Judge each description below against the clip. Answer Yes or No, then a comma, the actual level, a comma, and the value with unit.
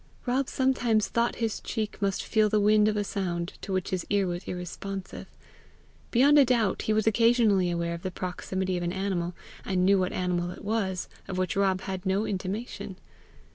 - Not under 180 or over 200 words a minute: Yes, average, 190 wpm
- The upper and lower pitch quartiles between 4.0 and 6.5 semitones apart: No, average, 2.9 semitones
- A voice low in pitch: No, high, 195 Hz